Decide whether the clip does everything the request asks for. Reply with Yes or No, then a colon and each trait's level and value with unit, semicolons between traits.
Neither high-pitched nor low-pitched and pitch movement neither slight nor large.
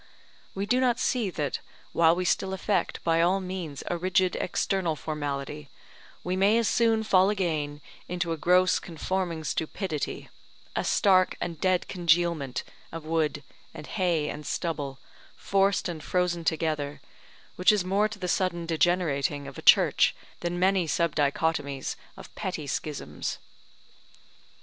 Yes: medium, 170 Hz; average, 3.5 semitones